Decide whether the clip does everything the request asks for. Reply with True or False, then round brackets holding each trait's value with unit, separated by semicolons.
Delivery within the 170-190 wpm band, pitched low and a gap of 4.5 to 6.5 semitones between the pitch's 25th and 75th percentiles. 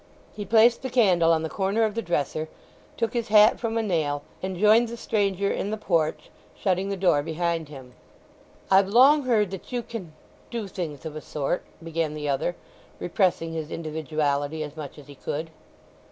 False (180 wpm; 175 Hz; 5.4 semitones)